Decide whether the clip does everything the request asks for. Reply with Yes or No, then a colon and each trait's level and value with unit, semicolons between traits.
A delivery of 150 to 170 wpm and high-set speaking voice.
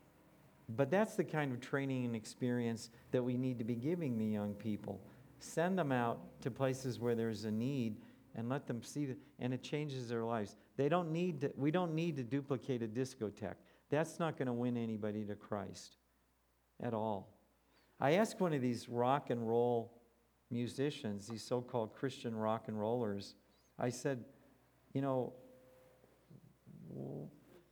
No: average, 165 wpm; low, 125 Hz